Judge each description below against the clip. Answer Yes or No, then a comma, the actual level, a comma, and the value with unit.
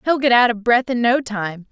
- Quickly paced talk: Yes, fast, 280 wpm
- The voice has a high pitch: Yes, high, 235 Hz